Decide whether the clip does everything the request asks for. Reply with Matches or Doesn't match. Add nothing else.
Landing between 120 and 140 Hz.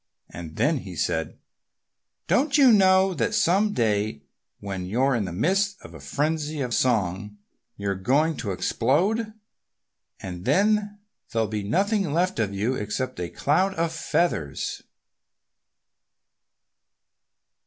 Matches